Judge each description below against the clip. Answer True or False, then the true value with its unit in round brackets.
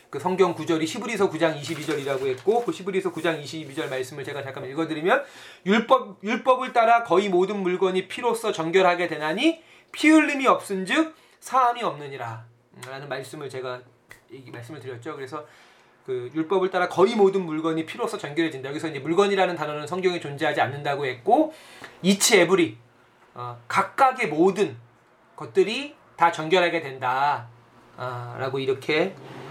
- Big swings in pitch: True (6.5 semitones)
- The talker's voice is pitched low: False (170 Hz)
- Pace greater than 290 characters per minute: True (325 characters per minute)